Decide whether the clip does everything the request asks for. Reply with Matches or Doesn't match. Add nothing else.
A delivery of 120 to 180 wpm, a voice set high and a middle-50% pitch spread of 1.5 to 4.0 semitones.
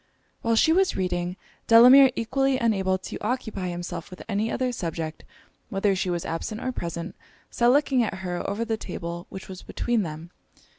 Doesn't match